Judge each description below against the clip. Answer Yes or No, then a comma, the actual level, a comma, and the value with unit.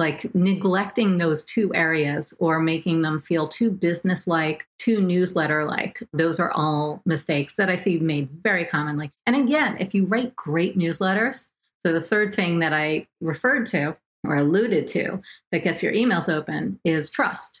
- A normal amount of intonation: Yes, average, 4.2 semitones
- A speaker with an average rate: Yes, average, 170 wpm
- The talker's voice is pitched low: No, medium, 170 Hz